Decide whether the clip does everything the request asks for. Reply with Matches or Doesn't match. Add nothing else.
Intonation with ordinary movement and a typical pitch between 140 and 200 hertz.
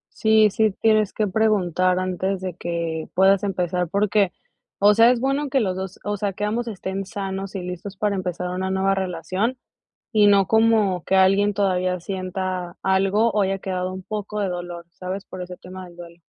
Doesn't match